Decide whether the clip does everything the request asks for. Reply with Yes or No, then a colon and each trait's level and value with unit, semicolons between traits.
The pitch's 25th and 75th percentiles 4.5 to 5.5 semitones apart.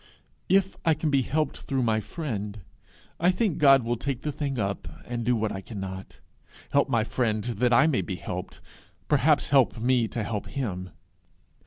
Yes: average, 4.8 semitones